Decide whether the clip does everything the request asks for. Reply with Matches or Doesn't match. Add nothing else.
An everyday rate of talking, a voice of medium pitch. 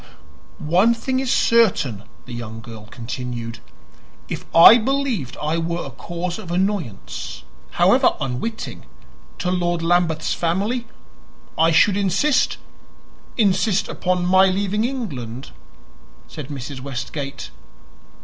Doesn't match